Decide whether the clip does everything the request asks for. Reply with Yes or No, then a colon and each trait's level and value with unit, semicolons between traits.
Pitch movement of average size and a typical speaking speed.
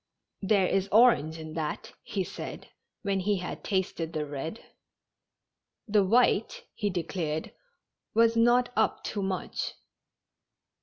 No: average, 5.0 semitones; slow, 120 wpm